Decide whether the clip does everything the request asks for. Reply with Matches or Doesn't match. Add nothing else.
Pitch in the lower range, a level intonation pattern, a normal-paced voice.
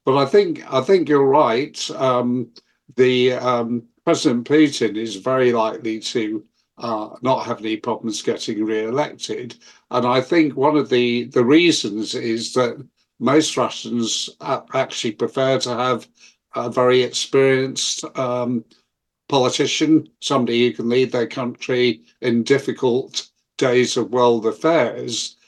Doesn't match